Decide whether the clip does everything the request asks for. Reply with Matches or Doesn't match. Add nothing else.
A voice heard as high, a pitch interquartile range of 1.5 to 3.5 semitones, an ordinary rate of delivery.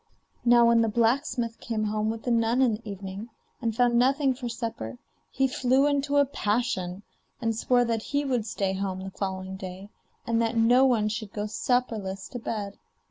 Matches